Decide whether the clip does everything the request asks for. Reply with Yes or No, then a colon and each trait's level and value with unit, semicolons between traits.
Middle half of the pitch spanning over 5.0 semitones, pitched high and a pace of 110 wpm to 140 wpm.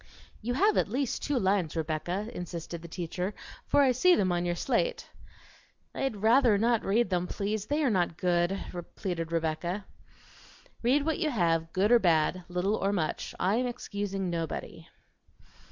No: wide, 5.6 semitones; high, 195 Hz; average, 165 wpm